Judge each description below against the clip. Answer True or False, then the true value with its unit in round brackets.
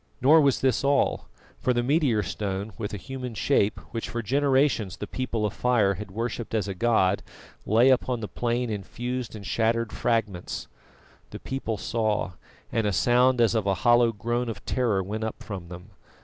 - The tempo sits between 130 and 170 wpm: False (185 wpm)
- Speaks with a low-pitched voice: True (115 Hz)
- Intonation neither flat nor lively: True (3.2 semitones)